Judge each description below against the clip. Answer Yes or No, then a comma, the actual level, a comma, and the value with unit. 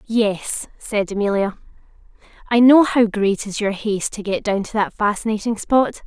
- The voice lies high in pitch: Yes, high, 210 Hz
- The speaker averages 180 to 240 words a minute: No, average, 170 wpm